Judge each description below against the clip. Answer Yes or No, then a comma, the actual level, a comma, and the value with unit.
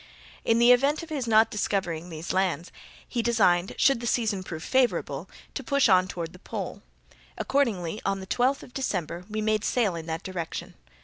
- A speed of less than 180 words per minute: No, average, 185 wpm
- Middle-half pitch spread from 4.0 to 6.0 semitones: Yes, average, 5.2 semitones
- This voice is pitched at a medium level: No, high, 210 Hz